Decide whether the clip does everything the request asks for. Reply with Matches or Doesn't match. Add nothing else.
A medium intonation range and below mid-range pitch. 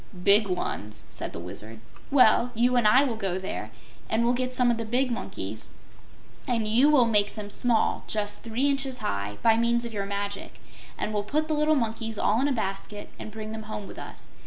Doesn't match